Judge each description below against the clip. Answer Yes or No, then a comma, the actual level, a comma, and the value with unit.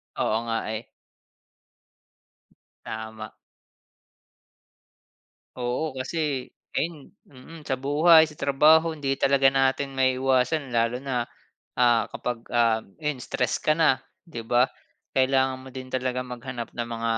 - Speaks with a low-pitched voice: Yes, low, 130 Hz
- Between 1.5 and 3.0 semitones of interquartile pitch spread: Yes, narrow, 2.5 semitones